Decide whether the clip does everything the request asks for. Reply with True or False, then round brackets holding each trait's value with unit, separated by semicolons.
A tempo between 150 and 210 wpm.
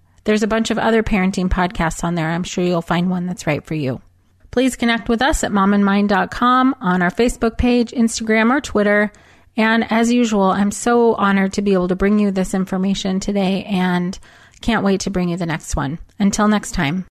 True (205 wpm)